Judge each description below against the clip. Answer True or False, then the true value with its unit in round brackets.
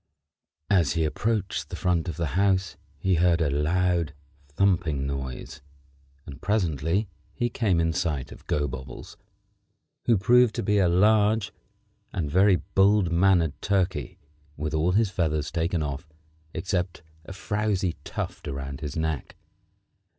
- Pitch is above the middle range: False (90 Hz)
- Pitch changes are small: False (4.3 semitones)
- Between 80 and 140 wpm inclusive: True (135 wpm)